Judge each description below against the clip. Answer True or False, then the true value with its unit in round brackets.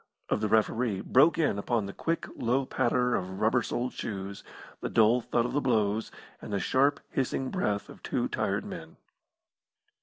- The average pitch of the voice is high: False (120 Hz)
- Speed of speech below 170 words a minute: False (175 wpm)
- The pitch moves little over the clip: False (3.8 semitones)